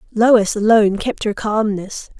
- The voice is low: No, high, 215 Hz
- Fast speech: No, slow, 135 wpm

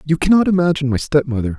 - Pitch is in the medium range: Yes, medium, 150 Hz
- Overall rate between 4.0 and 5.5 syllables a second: No, 7.8 syllables/s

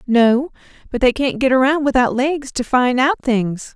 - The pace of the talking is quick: No, average, 190 wpm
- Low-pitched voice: No, very high, 255 Hz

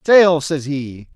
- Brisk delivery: No, average, 155 wpm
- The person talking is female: No, male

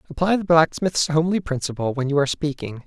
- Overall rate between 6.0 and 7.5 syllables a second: Yes, 6.4 syllables/s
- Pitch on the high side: No, medium, 155 Hz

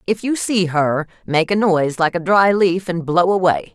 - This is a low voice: No, medium, 180 Hz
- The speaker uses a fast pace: Yes, fast, 225 wpm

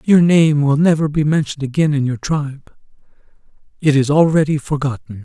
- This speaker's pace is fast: No, average, 150 wpm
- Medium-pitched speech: Yes, medium, 145 Hz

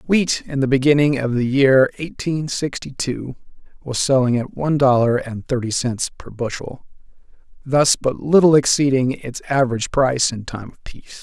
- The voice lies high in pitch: No, low, 130 Hz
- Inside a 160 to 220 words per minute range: Yes, average, 165 wpm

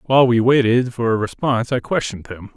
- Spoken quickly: Yes, fast, 210 wpm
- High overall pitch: No, low, 120 Hz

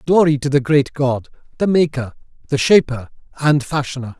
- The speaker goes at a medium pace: Yes, average, 155 wpm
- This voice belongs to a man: Yes, male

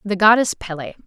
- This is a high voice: Yes, high, 200 Hz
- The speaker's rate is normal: Yes, average, 170 wpm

